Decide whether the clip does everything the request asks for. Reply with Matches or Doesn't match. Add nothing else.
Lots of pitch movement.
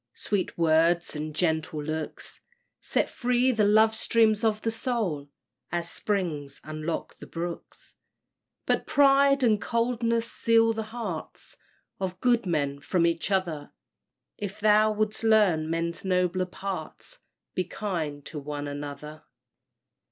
Matches